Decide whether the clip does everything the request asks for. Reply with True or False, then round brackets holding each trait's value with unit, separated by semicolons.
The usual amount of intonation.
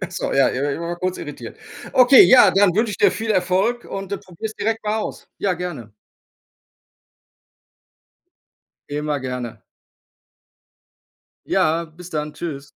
False (5.7 semitones)